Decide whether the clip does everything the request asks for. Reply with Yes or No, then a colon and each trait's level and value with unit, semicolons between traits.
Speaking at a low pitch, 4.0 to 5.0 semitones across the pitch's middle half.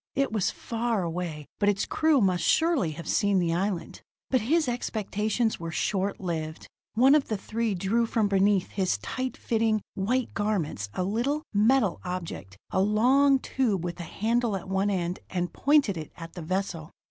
No: high, 200 Hz; average, 4.7 semitones